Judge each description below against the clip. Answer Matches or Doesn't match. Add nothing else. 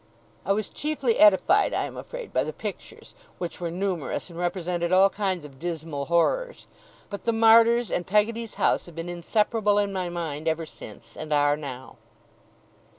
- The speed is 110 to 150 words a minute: Doesn't match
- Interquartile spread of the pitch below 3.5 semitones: Doesn't match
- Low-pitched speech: Doesn't match